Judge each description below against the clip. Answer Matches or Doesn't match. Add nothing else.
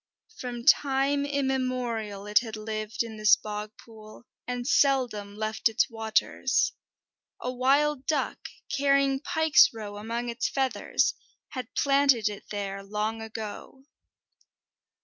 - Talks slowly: Matches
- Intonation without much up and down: Doesn't match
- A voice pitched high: Matches